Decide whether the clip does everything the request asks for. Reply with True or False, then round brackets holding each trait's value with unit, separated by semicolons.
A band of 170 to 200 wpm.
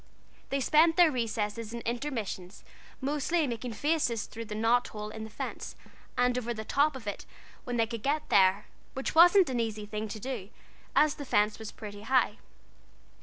True (185 wpm)